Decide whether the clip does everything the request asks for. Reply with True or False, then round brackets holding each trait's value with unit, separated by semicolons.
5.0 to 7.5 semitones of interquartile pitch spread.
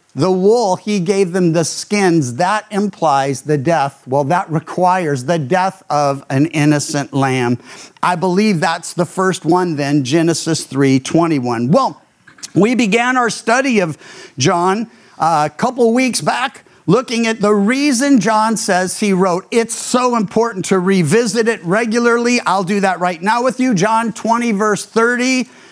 True (5.6 semitones)